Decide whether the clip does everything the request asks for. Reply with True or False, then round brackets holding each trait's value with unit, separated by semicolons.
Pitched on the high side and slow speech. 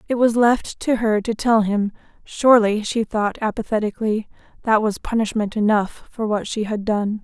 False (215 Hz; 175 wpm)